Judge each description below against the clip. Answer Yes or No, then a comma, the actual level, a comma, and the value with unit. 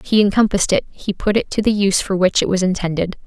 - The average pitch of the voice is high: Yes, high, 195 Hz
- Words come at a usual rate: No, fast, 275 wpm